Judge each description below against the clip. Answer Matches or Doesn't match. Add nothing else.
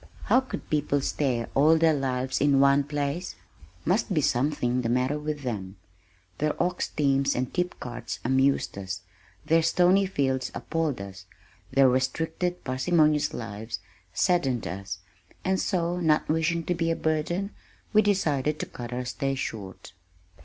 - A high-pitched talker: Doesn't match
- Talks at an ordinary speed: Matches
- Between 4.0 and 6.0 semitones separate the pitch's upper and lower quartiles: Matches